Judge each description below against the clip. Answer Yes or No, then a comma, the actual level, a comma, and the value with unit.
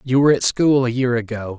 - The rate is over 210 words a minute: Yes, fast, 265 wpm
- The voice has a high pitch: No, low, 125 Hz